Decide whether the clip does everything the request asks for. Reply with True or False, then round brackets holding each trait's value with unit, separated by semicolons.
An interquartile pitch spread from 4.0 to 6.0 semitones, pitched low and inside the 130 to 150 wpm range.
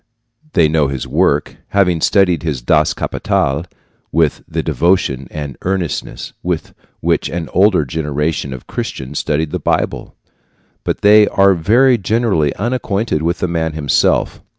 True (4.7 semitones; 80 Hz; 140 wpm)